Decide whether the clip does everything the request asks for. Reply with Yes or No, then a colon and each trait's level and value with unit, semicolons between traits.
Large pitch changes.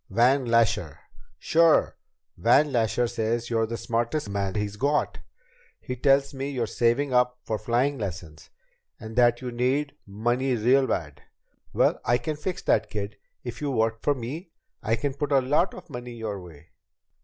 No: average, 3.6 semitones